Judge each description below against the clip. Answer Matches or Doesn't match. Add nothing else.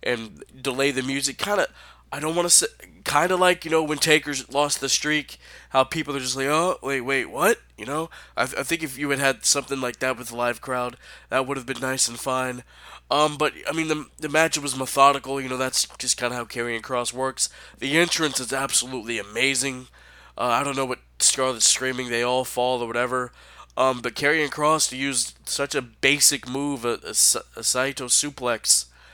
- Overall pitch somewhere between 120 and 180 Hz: Matches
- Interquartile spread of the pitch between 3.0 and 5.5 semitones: Doesn't match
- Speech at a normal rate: Doesn't match